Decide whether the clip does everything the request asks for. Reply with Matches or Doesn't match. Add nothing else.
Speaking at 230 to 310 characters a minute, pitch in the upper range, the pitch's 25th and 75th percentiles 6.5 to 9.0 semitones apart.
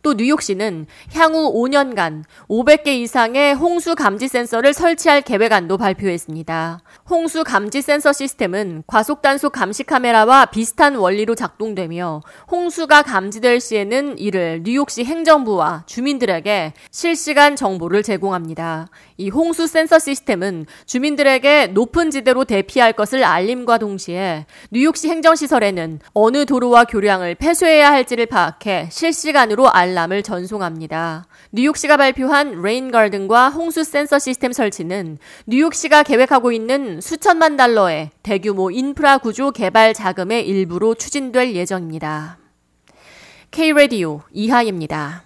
Doesn't match